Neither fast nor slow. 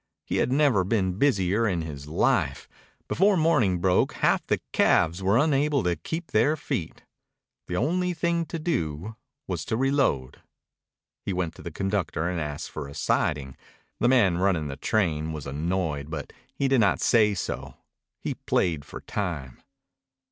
Yes: average, 160 wpm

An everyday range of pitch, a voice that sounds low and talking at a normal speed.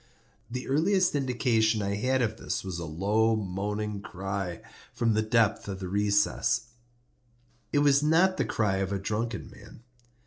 Yes: average, 4.1 semitones; low, 110 Hz; average, 160 wpm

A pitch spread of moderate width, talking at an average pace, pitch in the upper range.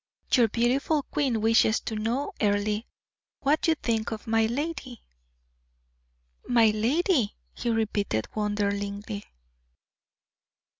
No: average, 3.3 semitones; slow, 100 wpm; high, 225 Hz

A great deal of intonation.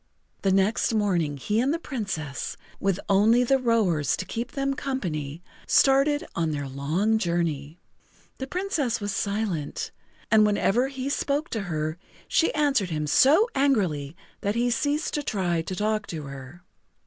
Yes: wide, 8.1 semitones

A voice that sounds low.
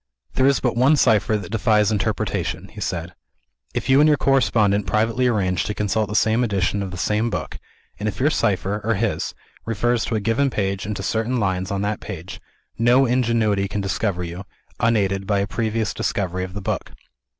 Yes: low, 105 Hz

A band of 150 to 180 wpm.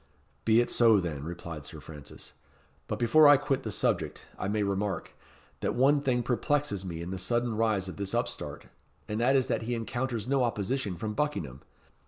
No: average, 190 wpm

